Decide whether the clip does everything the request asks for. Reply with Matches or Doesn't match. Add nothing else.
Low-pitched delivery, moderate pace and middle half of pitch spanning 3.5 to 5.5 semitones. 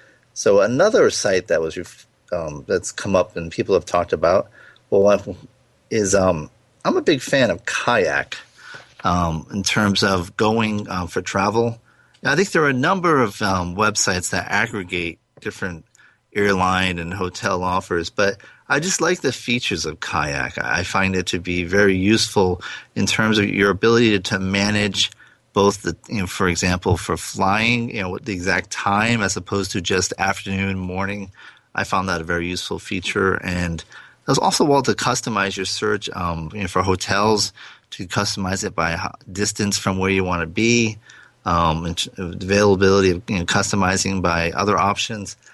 Doesn't match